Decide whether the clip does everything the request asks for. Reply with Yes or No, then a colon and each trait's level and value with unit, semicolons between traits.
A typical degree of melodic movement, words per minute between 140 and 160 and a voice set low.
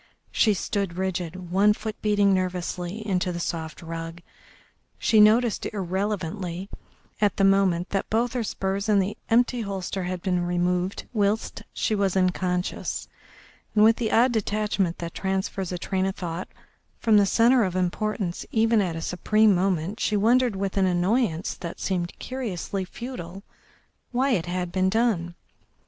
No: average, 3.0 semitones; average, 155 wpm; high, 195 Hz